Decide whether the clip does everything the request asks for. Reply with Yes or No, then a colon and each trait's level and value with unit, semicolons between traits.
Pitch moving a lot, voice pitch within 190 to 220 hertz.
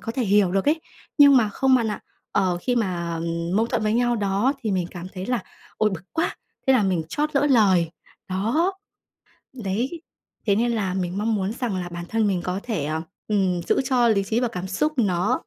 No: average, 4.6 semitones; high, 205 Hz